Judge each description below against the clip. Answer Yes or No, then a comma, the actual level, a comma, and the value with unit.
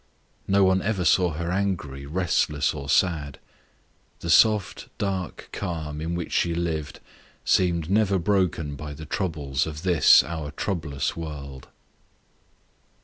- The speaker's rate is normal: No, slow, 130 wpm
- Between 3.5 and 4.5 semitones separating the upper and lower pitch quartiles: Yes, average, 3.9 semitones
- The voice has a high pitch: No, very low, 85 Hz